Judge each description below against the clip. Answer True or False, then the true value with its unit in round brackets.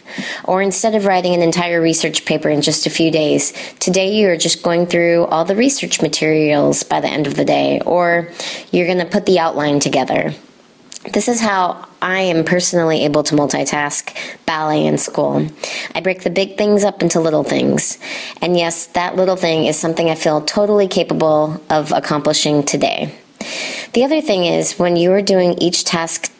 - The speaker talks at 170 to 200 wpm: True (185 wpm)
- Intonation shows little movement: False (3.3 semitones)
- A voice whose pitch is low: False (170 Hz)